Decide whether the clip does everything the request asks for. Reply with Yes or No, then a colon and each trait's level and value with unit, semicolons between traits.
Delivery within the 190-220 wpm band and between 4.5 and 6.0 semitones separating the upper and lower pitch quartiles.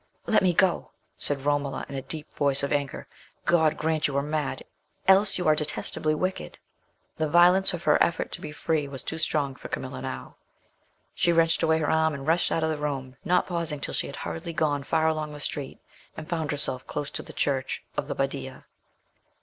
No: fast, 205 wpm; narrow, 2.4 semitones